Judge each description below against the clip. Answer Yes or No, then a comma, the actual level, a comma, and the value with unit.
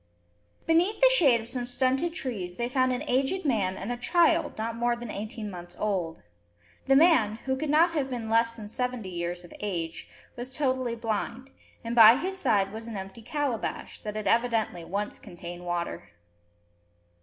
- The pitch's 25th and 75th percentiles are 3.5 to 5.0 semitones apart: Yes, average, 4.3 semitones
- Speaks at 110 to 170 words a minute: No, average, 180 wpm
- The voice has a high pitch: Yes, high, 235 Hz